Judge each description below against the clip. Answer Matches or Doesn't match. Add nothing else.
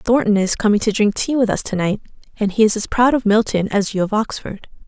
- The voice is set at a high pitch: Matches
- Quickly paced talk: Matches